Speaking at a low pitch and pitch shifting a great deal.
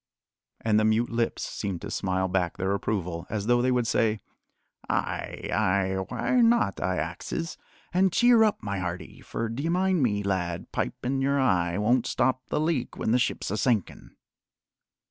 Yes: low, 110 Hz; wide, 5.7 semitones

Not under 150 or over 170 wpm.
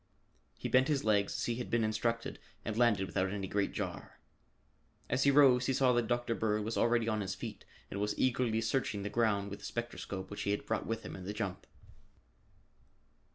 No: fast, 205 wpm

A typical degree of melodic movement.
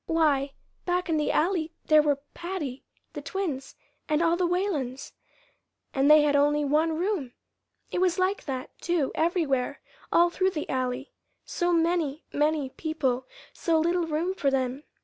Yes: average, 3.9 semitones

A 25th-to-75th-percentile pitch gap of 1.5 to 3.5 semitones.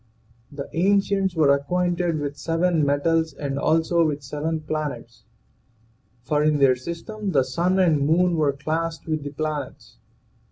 Yes: average, 3.1 semitones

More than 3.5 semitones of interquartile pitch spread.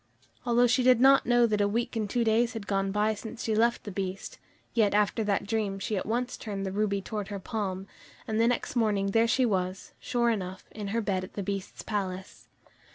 No: average, 2.9 semitones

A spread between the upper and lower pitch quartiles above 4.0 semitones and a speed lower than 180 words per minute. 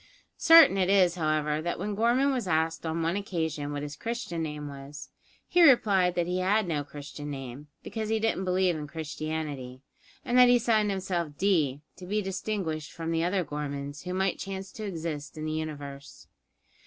No: average, 4.8 semitones; average, 185 wpm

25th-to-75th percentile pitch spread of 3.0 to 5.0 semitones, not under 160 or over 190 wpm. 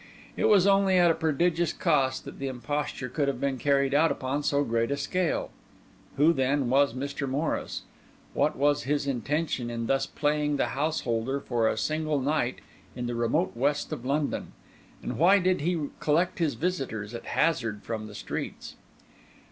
Yes: average, 3.5 semitones; average, 170 wpm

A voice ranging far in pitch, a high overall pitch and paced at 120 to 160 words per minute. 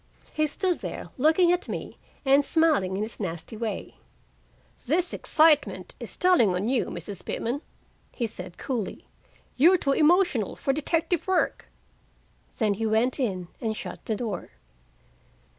Yes: wide, 7.0 semitones; very high, 260 Hz; average, 140 wpm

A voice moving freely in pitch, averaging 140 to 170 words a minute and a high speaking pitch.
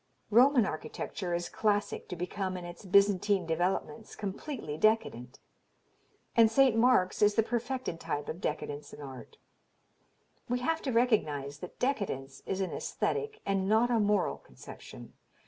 Yes: wide, 5.7 semitones; average, 145 wpm; high, 200 Hz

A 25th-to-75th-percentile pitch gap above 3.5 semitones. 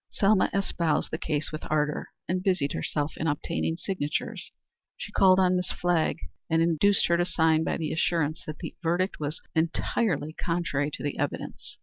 No: average, 3.0 semitones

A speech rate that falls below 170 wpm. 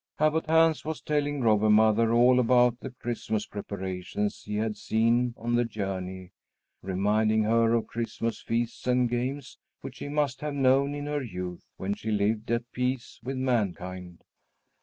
Yes: average, 160 wpm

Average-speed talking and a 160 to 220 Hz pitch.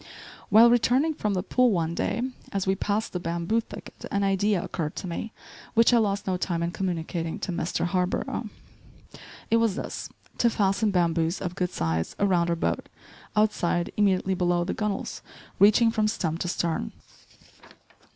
Yes: average, 165 wpm; high, 190 Hz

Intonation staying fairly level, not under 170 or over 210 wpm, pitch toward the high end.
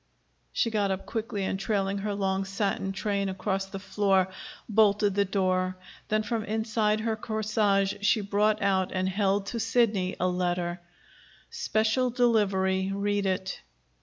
No: narrow, 2.1 semitones; average, 145 wpm; high, 200 Hz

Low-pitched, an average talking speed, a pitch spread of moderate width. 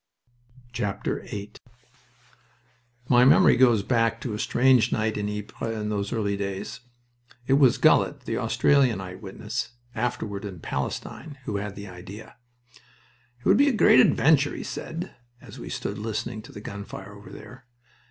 Yes: low, 110 Hz; average, 150 wpm; average, 3.4 semitones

